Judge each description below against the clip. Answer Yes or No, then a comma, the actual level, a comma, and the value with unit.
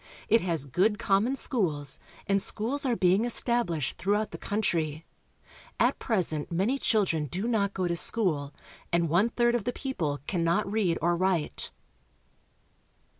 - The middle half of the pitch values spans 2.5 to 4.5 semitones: No, average, 5.0 semitones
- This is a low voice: No, high, 190 Hz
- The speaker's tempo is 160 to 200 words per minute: No, average, 150 wpm